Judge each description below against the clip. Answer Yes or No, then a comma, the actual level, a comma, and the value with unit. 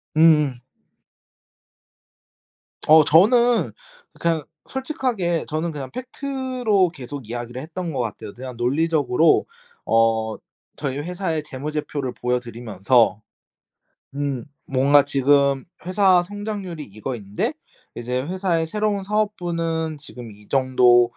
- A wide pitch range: Yes, wide, 6.3 semitones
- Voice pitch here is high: No, medium, 150 Hz